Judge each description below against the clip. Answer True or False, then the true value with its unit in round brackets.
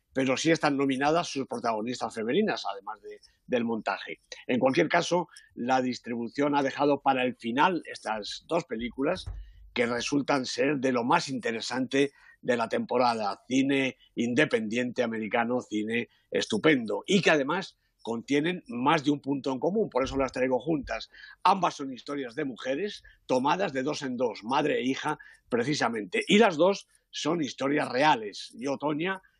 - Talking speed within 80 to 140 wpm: False (155 wpm)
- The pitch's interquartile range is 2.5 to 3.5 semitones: False (4.0 semitones)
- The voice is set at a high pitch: False (135 Hz)